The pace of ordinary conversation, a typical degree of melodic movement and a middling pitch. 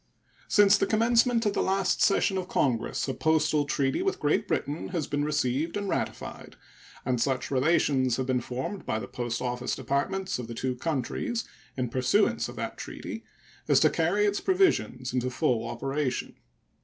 No: average, 170 wpm; wide, 7.3 semitones; medium, 145 Hz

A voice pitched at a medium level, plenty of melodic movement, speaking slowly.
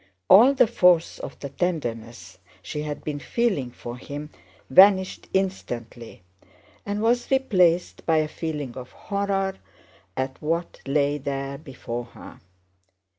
Yes: medium, 150 Hz; wide, 6.4 semitones; slow, 125 wpm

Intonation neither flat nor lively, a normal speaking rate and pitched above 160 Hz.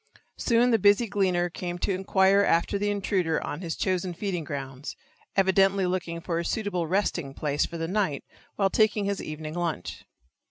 Yes: average, 3.2 semitones; average, 170 wpm; medium, 185 Hz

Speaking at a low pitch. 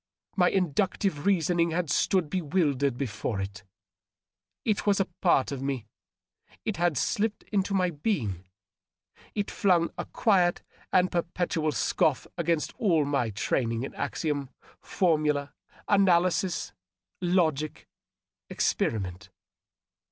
No: medium, 165 Hz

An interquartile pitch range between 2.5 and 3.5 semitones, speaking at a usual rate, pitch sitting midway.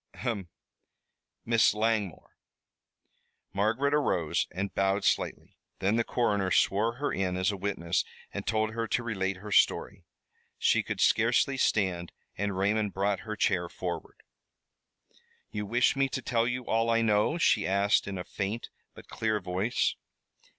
No: average, 2.9 semitones; average, 145 wpm; low, 105 Hz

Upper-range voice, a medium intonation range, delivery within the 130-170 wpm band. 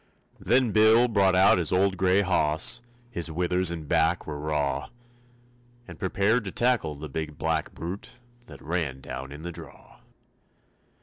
No: very low, 85 Hz; average, 4.2 semitones; average, 150 wpm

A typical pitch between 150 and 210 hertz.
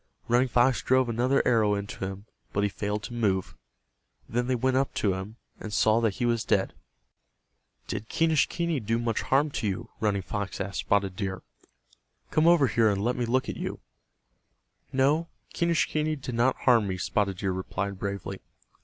No: low, 115 Hz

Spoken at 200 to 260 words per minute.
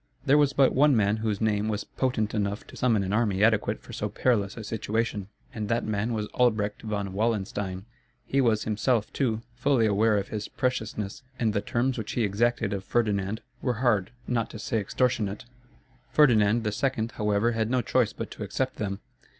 No: average, 185 wpm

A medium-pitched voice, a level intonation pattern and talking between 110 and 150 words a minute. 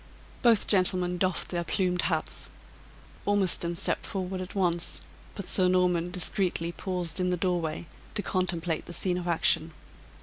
Yes: medium, 180 Hz; narrow, 1.4 semitones; average, 145 wpm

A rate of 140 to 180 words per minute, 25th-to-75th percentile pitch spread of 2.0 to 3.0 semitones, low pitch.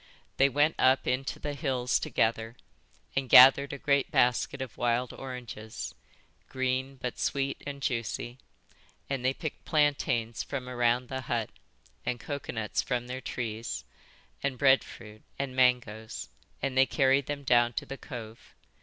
Yes: average, 145 wpm; narrow, 2.4 semitones; low, 130 Hz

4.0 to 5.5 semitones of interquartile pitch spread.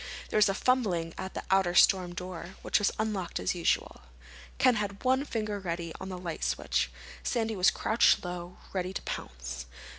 No: average, 3.4 semitones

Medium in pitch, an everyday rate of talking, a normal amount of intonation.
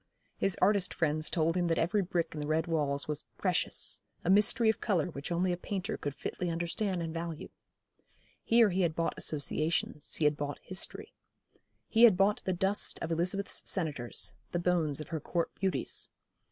Yes: medium, 170 Hz; average, 180 wpm; average, 3.4 semitones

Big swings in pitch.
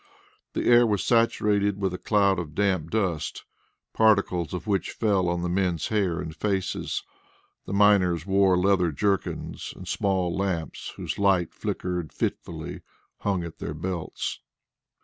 No: narrow, 2.6 semitones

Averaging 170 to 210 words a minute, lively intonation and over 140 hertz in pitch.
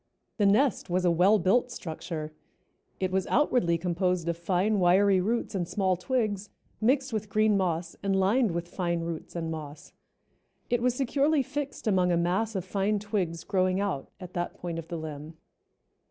No: average, 175 wpm; average, 3.8 semitones; medium, 185 Hz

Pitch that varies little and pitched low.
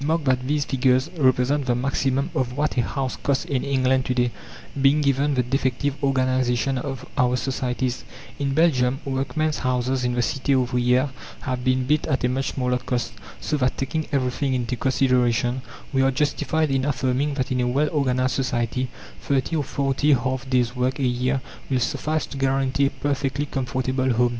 Yes: narrow, 1.6 semitones; low, 130 Hz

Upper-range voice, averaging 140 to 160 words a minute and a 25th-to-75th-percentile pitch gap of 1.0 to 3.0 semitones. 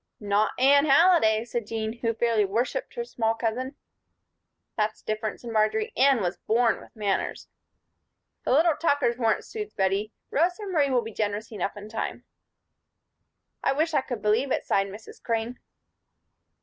No: high, 230 Hz; average, 155 wpm; average, 4.1 semitones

